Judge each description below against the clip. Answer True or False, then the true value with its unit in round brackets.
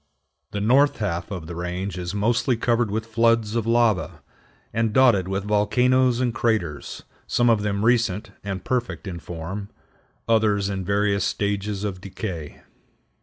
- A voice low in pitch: True (105 Hz)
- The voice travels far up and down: False (3.1 semitones)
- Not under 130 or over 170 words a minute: True (150 wpm)